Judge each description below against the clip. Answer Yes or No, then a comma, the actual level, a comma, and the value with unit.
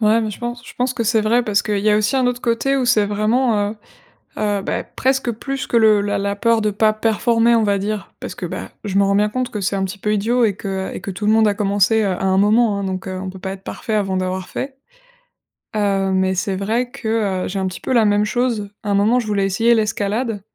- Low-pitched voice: No, high, 210 Hz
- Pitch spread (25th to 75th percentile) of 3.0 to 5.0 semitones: No, narrow, 2.6 semitones